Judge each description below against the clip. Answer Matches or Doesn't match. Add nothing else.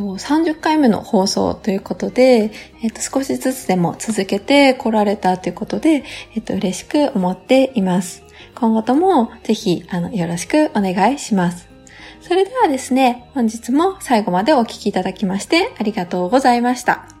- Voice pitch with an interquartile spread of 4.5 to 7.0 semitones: Matches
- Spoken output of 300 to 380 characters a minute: Matches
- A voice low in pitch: Doesn't match